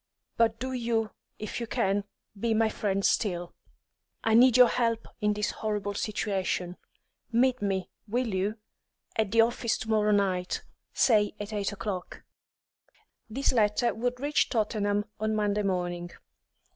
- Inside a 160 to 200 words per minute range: No, average, 145 wpm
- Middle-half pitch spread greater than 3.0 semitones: No, narrow, 2.4 semitones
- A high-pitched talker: Yes, high, 215 Hz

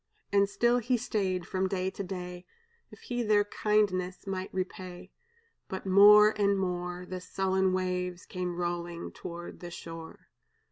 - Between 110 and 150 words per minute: Yes, average, 145 wpm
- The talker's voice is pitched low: No, medium, 185 Hz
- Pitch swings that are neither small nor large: No, narrow, 2.0 semitones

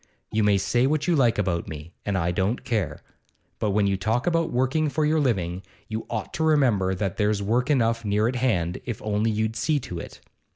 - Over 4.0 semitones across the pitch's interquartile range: Yes, average, 4.7 semitones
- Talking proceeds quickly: Yes, fast, 215 wpm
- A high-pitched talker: No, low, 110 Hz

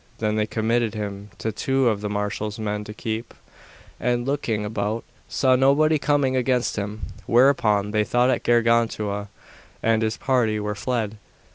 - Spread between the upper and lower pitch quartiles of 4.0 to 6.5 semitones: No, average, 3.0 semitones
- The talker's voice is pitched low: Yes, low, 110 Hz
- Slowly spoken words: No, average, 155 wpm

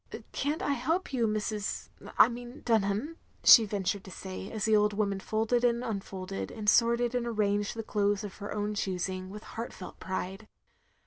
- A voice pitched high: Yes, high, 210 Hz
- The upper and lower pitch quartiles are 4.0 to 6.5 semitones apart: No, average, 2.9 semitones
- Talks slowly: No, average, 180 wpm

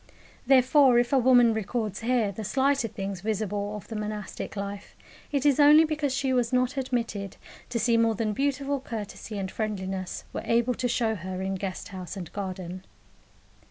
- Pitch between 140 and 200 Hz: No, high, 225 Hz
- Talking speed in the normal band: Yes, average, 175 wpm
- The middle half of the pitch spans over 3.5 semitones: Yes, average, 4.3 semitones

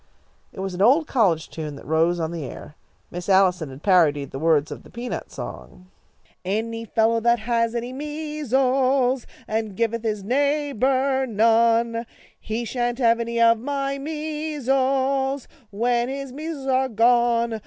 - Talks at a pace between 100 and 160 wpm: Yes, average, 155 wpm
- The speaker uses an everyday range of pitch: Yes, average, 4.3 semitones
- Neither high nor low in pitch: No, high, 235 Hz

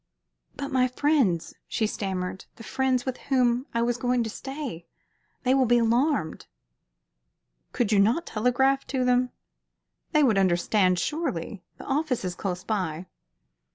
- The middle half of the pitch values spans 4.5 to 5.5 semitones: Yes, average, 5.2 semitones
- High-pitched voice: Yes, high, 240 Hz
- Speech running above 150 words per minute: No, average, 145 wpm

